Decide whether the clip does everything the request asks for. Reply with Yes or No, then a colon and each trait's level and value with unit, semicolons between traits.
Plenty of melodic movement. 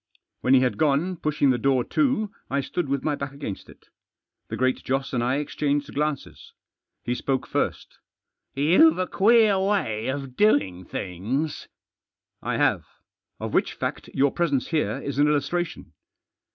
No: average, 4.4 semitones